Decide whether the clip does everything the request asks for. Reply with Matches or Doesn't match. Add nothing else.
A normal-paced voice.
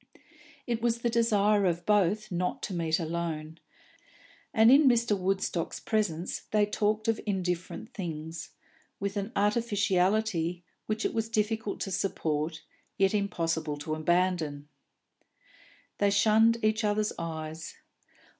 Doesn't match